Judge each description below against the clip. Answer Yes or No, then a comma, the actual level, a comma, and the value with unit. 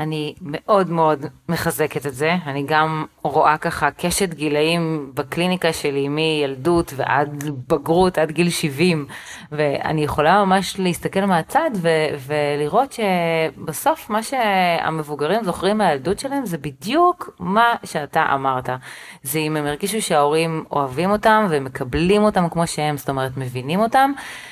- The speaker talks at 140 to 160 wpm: No, average, 130 wpm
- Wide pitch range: No, average, 4.0 semitones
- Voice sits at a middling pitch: Yes, medium, 160 Hz